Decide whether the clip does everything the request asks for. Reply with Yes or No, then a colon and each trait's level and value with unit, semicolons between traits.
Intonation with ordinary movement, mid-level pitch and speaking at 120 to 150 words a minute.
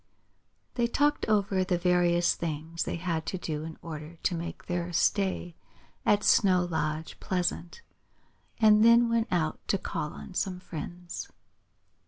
Yes: average, 3.1 semitones; medium, 175 Hz; average, 145 wpm